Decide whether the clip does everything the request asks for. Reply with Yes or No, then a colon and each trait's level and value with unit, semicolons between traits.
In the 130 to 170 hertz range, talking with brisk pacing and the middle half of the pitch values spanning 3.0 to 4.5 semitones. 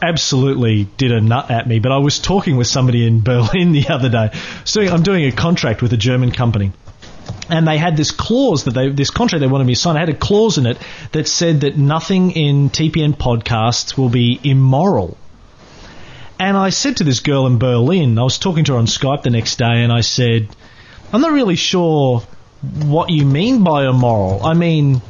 No: low, 135 Hz; fast, 210 wpm; wide, 5.4 semitones